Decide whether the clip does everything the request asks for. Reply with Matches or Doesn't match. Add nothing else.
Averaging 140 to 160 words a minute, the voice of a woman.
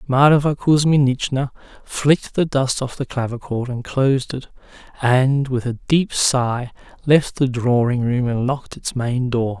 Doesn't match